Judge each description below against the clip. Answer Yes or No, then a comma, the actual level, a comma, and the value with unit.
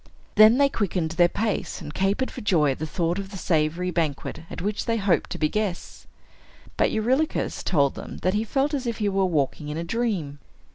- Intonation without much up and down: No, average, 5.3 semitones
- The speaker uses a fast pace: Yes, fast, 210 wpm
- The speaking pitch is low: No, high, 190 Hz